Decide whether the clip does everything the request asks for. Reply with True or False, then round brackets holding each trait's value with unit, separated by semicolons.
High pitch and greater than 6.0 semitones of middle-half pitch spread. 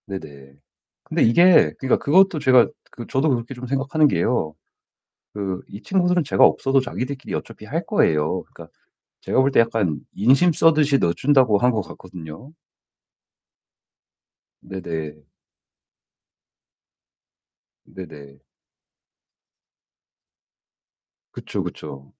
False (120 Hz; 8.0 semitones)